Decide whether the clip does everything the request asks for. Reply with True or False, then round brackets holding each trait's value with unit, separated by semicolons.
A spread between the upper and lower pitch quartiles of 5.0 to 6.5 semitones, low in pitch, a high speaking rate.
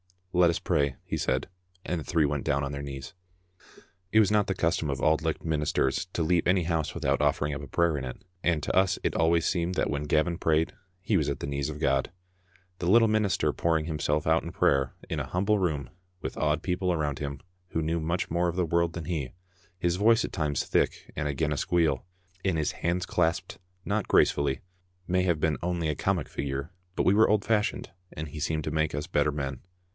False (3.2 semitones; 80 Hz; 225 wpm)